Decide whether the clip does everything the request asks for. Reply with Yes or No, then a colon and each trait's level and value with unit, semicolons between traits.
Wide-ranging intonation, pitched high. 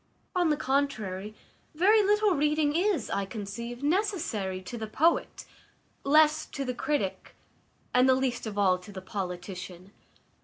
Yes: wide, 7.6 semitones; very high, 250 Hz